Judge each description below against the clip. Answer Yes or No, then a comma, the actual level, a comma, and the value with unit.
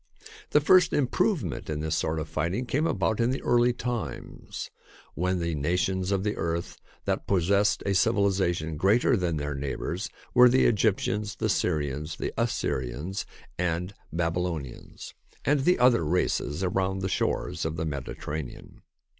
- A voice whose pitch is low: Yes, very low, 90 Hz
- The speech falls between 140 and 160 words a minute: Yes, average, 145 wpm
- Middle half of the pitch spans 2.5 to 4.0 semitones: No, wide, 5.4 semitones